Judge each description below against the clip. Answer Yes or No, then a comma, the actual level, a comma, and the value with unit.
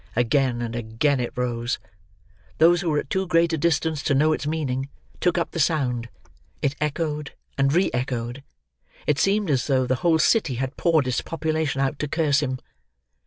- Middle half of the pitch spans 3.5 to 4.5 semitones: Yes, average, 4.0 semitones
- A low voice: No, medium, 145 Hz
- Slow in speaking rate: No, average, 185 wpm